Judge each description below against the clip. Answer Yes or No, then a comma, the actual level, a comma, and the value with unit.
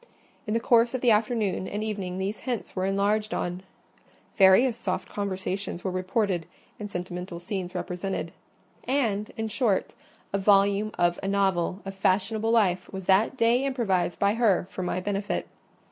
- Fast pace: No, average, 160 wpm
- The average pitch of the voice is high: Yes, high, 200 Hz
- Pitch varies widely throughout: No, average, 2.8 semitones